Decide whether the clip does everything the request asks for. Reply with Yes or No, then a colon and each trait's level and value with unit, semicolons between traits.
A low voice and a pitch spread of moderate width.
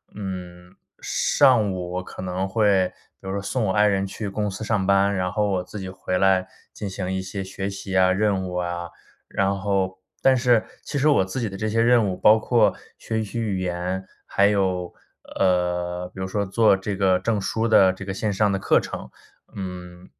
No: very low, 95 Hz; narrow, 2.1 semitones